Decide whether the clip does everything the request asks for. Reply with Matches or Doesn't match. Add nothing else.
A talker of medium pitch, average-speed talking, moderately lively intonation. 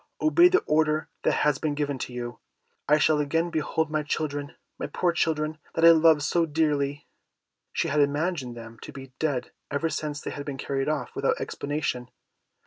Doesn't match